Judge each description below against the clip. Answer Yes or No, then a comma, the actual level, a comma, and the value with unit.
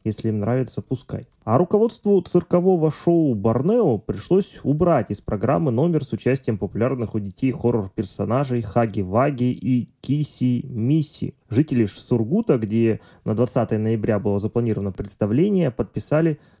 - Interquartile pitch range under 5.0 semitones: No, wide, 5.6 semitones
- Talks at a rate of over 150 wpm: No, average, 125 wpm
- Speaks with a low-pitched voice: Yes, low, 125 Hz